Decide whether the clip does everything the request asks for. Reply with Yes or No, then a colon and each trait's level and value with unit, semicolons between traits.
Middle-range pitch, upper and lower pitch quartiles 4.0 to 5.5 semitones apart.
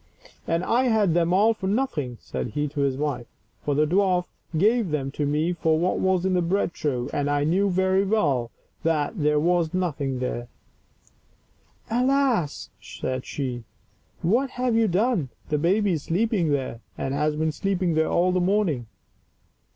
Yes: medium, 170 Hz; average, 5.1 semitones